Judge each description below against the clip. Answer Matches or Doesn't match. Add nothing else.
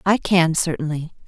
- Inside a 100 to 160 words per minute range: Matches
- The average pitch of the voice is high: Doesn't match